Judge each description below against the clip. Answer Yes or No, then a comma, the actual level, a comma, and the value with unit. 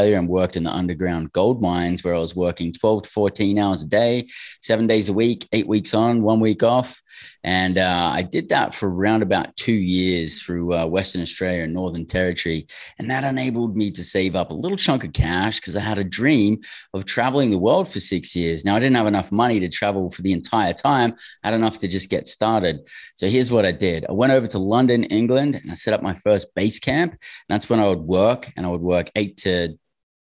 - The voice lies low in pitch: Yes, low, 100 Hz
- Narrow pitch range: No, average, 4.0 semitones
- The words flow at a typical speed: No, fast, 235 wpm